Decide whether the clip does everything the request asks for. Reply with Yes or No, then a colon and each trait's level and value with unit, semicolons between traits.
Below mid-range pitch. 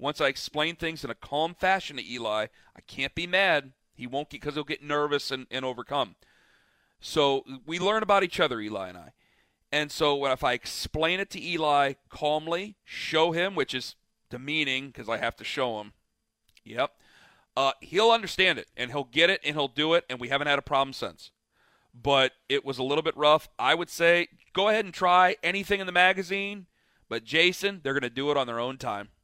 No: medium, 145 Hz